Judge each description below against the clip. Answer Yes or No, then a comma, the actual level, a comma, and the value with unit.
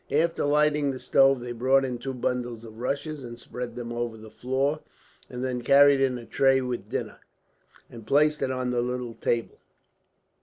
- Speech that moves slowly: No, average, 185 wpm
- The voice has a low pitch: Yes, low, 125 Hz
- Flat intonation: Yes, narrow, 2.3 semitones